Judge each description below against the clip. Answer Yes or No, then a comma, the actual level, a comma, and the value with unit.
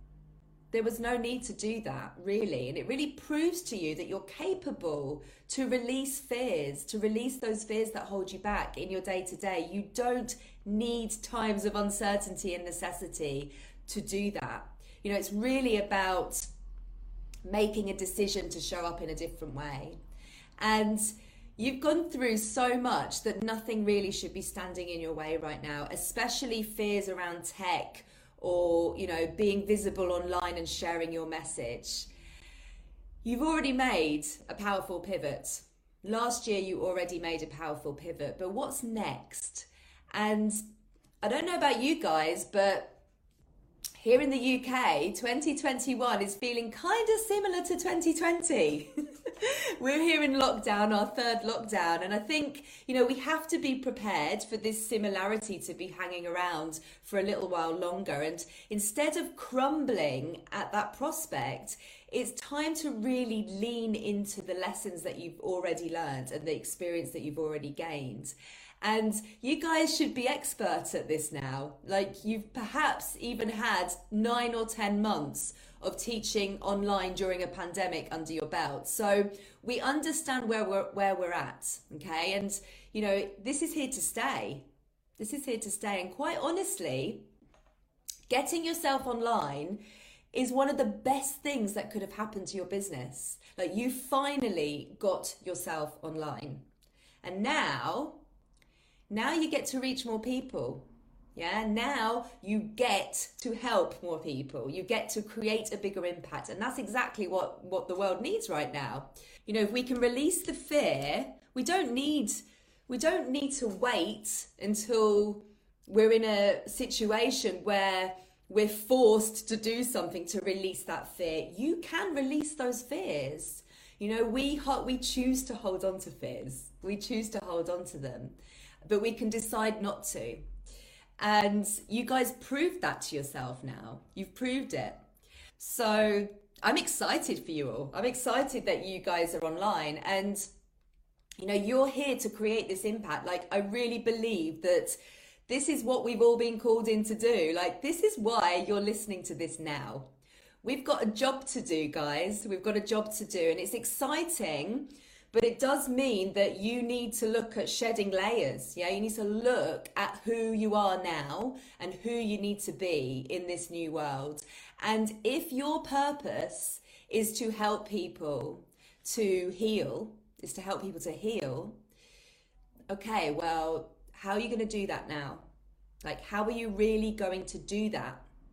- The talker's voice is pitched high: Yes, high, 215 Hz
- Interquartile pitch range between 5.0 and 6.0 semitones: Yes, wide, 5.5 semitones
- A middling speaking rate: Yes, average, 165 wpm